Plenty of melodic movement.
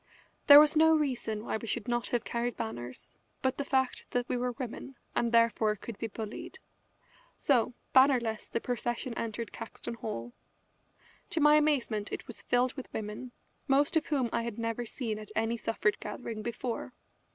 No: average, 2.9 semitones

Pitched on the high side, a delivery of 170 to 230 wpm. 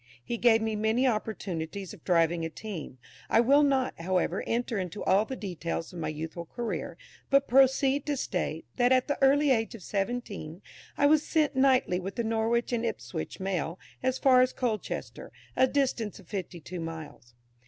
Yes: high, 220 Hz; average, 180 wpm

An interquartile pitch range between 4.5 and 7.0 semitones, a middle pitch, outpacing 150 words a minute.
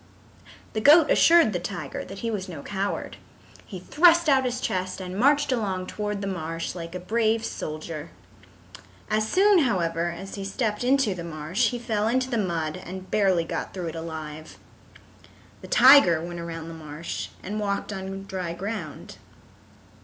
No: average, 5.2 semitones; high, 195 Hz; average, 170 wpm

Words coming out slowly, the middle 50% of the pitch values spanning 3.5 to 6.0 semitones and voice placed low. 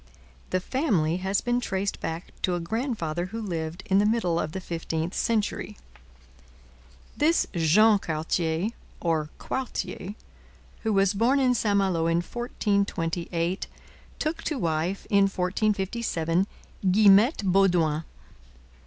No: slow, 120 wpm; average, 4.4 semitones; high, 190 Hz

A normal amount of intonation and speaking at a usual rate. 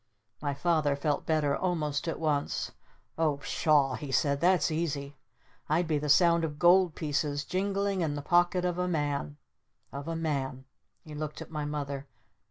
Yes: average, 3.0 semitones; average, 175 wpm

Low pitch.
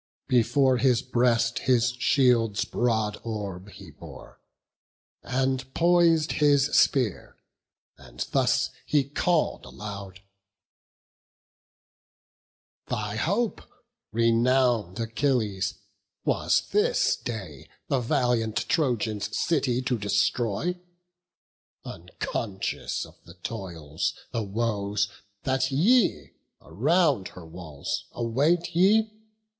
Yes: low, 120 Hz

